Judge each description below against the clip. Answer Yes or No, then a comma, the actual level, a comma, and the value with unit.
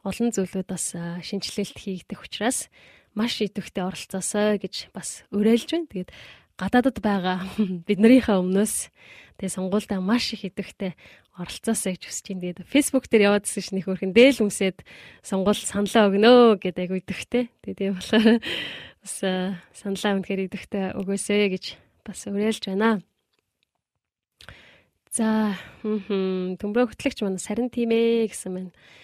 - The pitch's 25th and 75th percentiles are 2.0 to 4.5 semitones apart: Yes, average, 2.7 semitones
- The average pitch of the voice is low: No, high, 200 Hz